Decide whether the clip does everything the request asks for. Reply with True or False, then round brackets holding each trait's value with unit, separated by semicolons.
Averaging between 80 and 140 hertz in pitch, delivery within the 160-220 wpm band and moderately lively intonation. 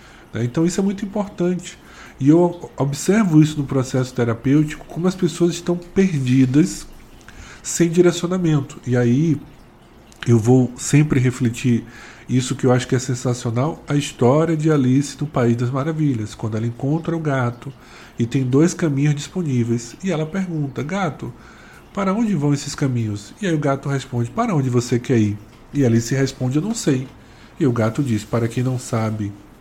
True (135 Hz; 170 wpm; 4.9 semitones)